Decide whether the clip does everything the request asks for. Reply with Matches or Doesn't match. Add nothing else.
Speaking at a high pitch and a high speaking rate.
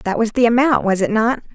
Matches